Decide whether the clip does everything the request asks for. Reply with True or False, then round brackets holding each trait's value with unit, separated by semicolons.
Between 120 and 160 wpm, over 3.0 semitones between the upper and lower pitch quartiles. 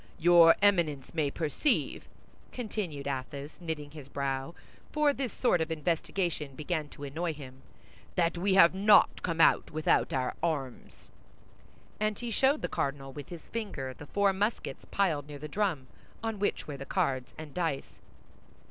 True (155 wpm; 5.3 semitones)